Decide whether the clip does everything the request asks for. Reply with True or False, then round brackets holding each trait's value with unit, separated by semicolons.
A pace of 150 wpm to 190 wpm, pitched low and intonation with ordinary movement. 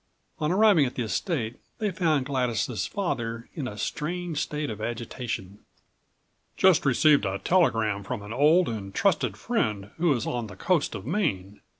False (165 wpm; 125 Hz; 7.1 semitones)